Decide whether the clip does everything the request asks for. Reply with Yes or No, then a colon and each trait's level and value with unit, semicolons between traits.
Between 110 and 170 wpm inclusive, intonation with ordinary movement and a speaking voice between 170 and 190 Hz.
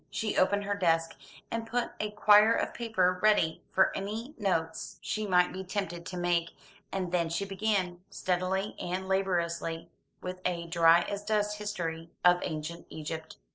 Yes: average, 160 wpm; average, 3.4 semitones; medium, 185 Hz